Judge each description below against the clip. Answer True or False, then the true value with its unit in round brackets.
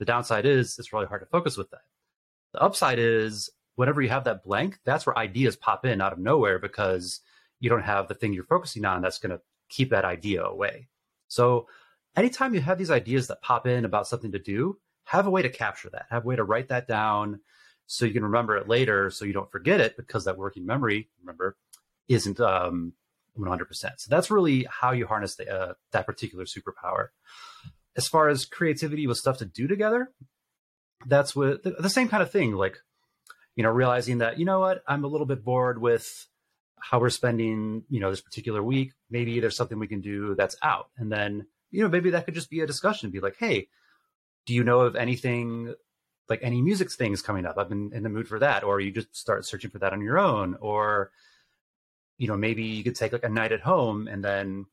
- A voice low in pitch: True (120 Hz)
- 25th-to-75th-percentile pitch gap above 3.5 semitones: True (4.2 semitones)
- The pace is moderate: False (220 wpm)